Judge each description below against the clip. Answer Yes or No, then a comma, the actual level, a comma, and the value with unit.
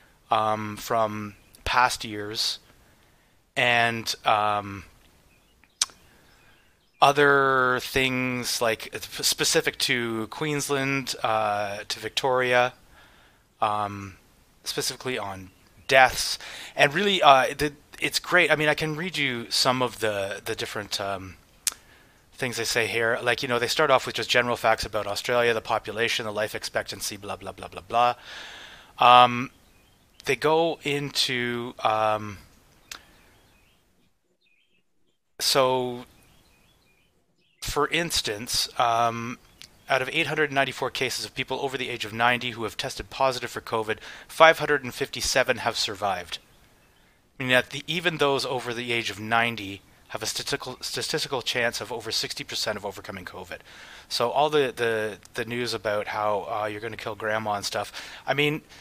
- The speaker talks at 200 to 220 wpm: No, slow, 135 wpm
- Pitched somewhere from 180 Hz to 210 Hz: No, low, 120 Hz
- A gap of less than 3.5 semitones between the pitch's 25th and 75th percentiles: No, average, 4.0 semitones